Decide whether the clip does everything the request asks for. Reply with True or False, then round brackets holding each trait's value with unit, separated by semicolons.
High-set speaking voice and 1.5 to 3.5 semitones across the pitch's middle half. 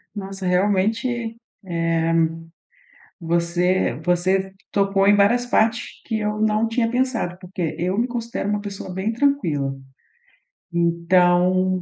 False (195 Hz; 3.9 semitones)